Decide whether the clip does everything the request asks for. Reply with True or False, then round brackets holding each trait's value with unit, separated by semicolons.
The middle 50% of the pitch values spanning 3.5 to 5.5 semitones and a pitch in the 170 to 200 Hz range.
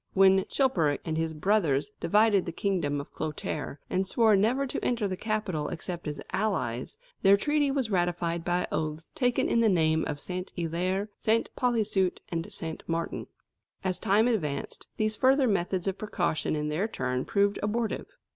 True (4.9 semitones; 190 Hz)